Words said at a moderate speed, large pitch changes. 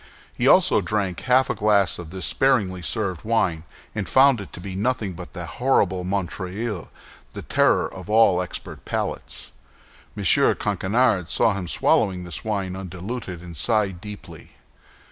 No: average, 145 wpm; average, 3.3 semitones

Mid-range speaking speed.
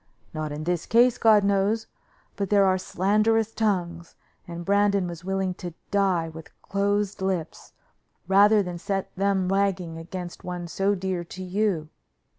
Yes: average, 150 wpm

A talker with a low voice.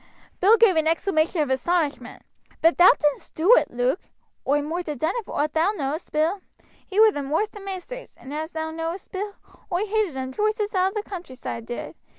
No: very high, 335 Hz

